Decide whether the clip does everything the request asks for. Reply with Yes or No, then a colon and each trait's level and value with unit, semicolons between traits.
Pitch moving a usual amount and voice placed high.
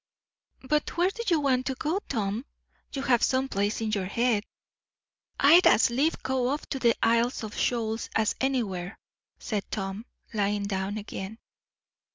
Yes: average, 4.4 semitones; high, 235 Hz